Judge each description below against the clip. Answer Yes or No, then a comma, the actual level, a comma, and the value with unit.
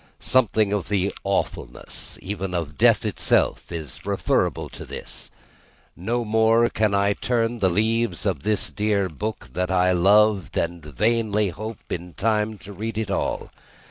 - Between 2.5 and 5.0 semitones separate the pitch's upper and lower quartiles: Yes, average, 3.2 semitones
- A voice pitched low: Yes, low, 105 Hz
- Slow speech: No, average, 150 wpm